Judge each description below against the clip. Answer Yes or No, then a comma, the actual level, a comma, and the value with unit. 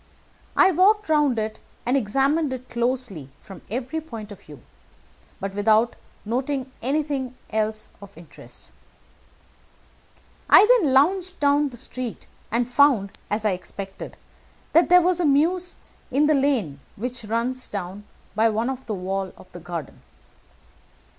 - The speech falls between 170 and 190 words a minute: No, slow, 135 wpm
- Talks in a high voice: Yes, high, 245 Hz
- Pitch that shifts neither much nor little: No, wide, 5.8 semitones